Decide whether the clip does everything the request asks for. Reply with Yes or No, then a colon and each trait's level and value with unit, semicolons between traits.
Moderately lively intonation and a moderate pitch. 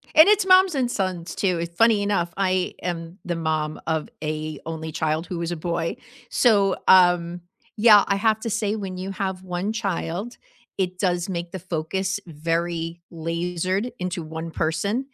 Yes: average, 3.1 semitones; medium, 180 Hz